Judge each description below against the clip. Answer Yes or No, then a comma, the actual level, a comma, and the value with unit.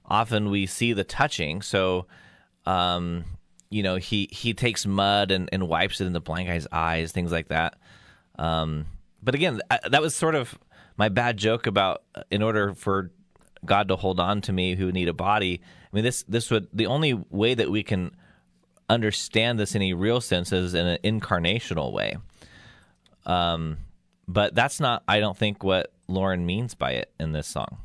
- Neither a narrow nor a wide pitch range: Yes, average, 3.5 semitones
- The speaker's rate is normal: Yes, average, 185 wpm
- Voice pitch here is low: Yes, very low, 95 Hz